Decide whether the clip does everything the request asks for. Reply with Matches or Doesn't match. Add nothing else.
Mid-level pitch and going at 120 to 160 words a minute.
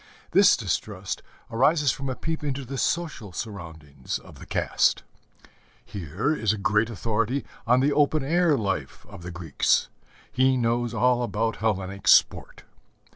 Doesn't match